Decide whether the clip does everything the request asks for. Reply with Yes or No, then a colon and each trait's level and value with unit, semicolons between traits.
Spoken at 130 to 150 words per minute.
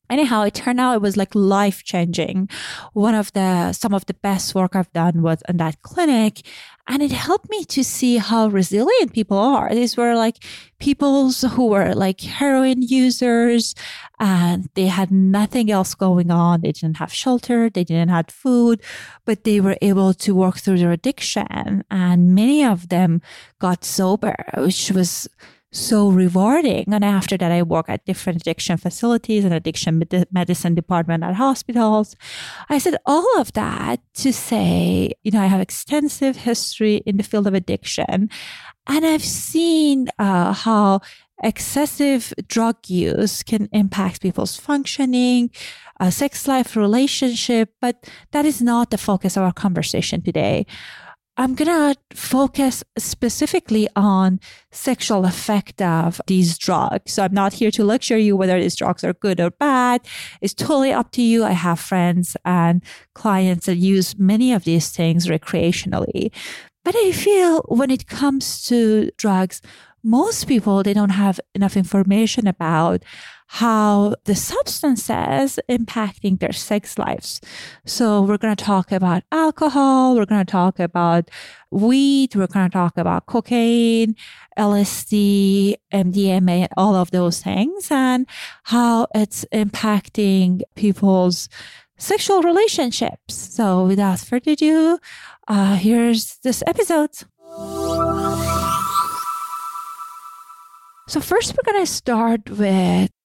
Yes: average, 140 wpm